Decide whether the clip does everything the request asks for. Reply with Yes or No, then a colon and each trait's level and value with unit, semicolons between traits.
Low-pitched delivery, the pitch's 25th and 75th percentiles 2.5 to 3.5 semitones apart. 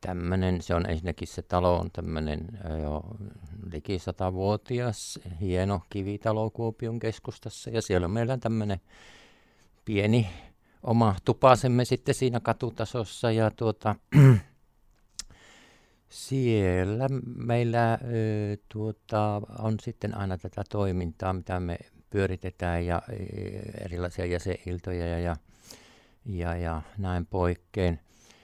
No: low, 100 Hz; average, 4.1 semitones